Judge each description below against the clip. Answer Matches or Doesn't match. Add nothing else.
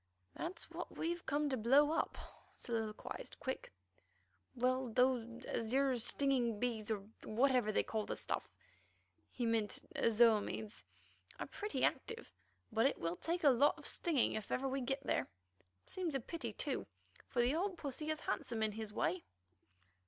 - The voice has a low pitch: Doesn't match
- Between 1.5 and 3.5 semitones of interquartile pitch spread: Doesn't match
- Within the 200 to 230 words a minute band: Doesn't match